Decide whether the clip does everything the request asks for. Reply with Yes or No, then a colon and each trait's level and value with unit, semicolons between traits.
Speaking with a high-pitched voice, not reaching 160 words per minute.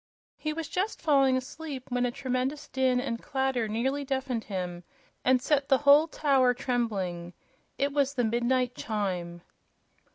Yes: very high, 255 Hz; average, 150 wpm